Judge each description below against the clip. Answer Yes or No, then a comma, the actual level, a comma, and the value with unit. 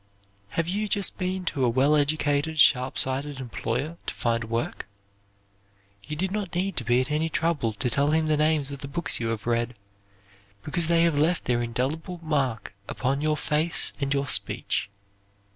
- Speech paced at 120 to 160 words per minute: No, average, 180 wpm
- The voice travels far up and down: No, average, 4.3 semitones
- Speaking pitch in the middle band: Yes, medium, 145 Hz